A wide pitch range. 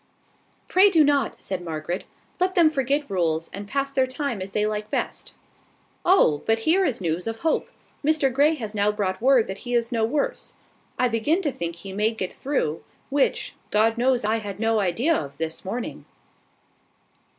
Yes: wide, 6.4 semitones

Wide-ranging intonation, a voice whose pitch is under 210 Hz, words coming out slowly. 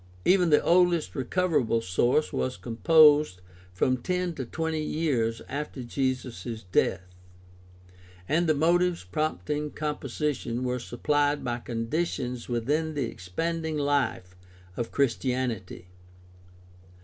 No: average, 4.8 semitones; medium, 140 Hz; slow, 110 wpm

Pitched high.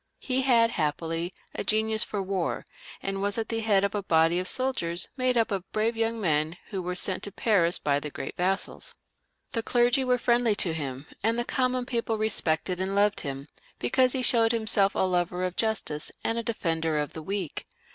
Yes: high, 200 Hz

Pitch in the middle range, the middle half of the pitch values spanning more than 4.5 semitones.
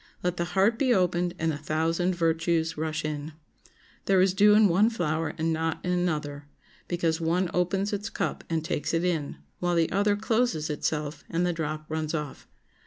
No: medium, 170 Hz; narrow, 2.6 semitones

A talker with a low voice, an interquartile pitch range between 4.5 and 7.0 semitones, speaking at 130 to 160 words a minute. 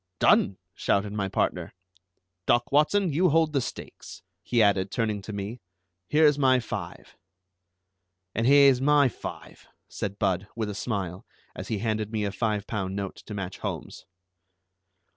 Yes: low, 110 Hz; average, 5.2 semitones; average, 150 wpm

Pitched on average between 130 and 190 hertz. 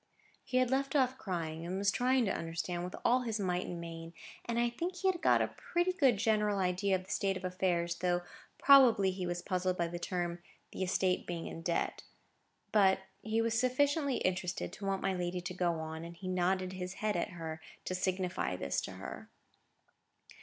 Yes: medium, 185 Hz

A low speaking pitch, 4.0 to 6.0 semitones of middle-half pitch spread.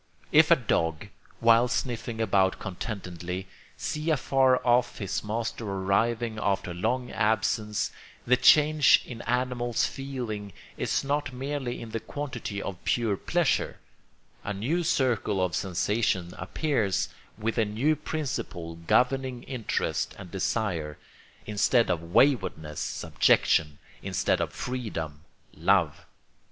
Yes: low, 115 Hz; average, 4.7 semitones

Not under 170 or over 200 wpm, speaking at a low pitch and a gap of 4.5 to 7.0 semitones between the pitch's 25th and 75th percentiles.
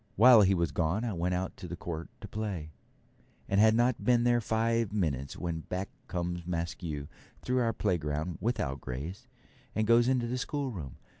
Yes: average, 175 wpm; very low, 95 Hz; wide, 5.6 semitones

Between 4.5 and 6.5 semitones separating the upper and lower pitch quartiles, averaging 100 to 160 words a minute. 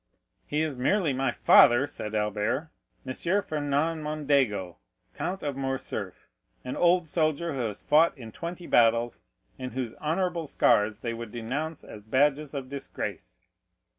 Yes: average, 5.0 semitones; slow, 135 wpm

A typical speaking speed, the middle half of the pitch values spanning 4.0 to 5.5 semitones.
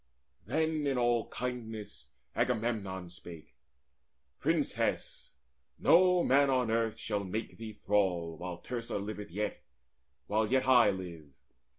No: slow, 115 wpm; average, 4.6 semitones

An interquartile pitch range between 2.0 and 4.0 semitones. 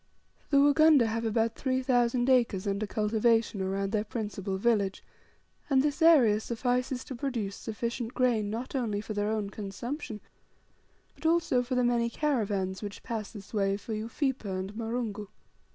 Yes: average, 3.4 semitones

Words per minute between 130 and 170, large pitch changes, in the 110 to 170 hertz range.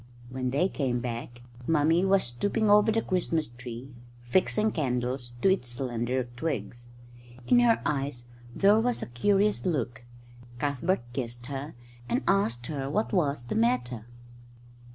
Yes: average, 140 wpm; wide, 7.5 semitones; low, 135 Hz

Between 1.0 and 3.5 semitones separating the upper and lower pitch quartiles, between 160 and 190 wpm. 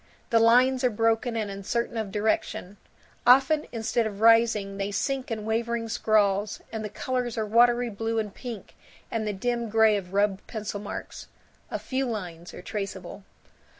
Yes: narrow, 2.5 semitones; average, 165 wpm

